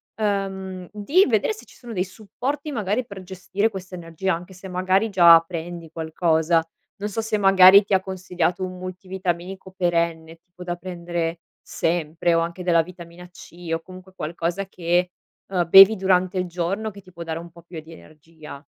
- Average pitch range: No, narrow, 2.3 semitones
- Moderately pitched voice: Yes, medium, 180 Hz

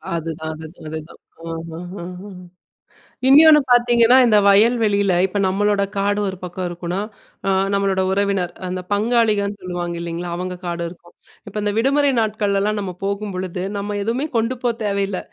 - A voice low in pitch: No, high, 200 Hz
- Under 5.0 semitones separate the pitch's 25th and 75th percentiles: Yes, average, 2.9 semitones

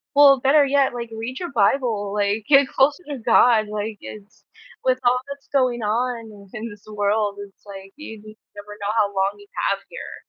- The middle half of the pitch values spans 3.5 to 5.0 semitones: Yes, average, 3.9 semitones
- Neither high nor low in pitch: No, high, 220 Hz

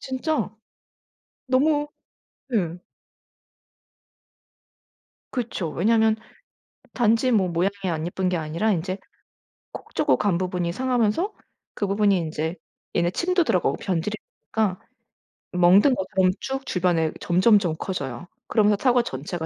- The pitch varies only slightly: No, average, 5.1 semitones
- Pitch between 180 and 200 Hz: Yes, high, 190 Hz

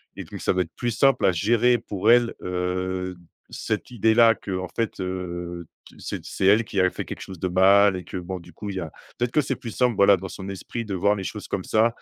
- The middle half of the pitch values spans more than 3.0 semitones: Yes, average, 3.6 semitones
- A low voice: Yes, very low, 95 Hz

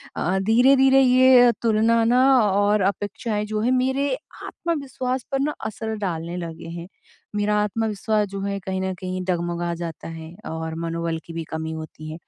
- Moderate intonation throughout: No, wide, 6.3 semitones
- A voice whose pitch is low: No, high, 205 Hz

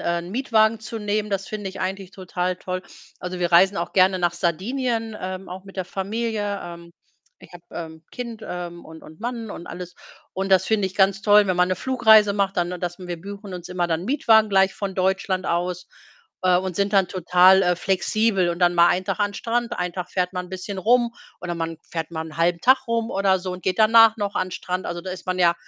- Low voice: No, medium, 185 Hz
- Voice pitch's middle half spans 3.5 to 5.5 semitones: No, narrow, 2.6 semitones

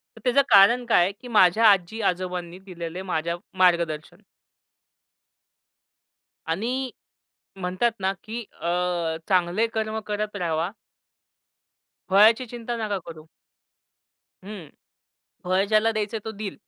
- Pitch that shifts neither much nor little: Yes, average, 4.0 semitones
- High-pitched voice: Yes, high, 195 Hz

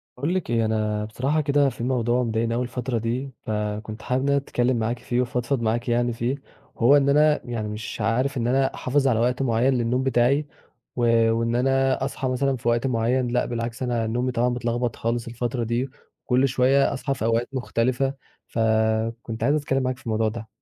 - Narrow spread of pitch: Yes, narrow, 2.3 semitones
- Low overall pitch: Yes, low, 120 Hz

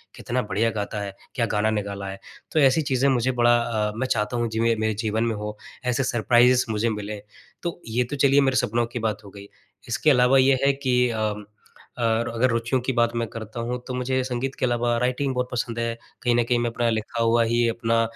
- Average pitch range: No, narrow, 2.2 semitones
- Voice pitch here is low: Yes, low, 120 Hz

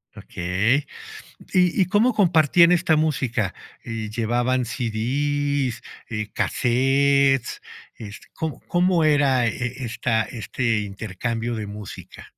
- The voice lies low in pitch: Yes, low, 125 Hz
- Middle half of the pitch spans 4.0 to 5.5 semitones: Yes, average, 4.6 semitones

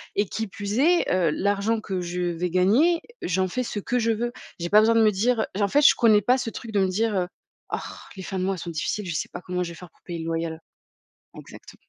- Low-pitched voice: No, high, 200 Hz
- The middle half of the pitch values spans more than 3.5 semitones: Yes, average, 3.9 semitones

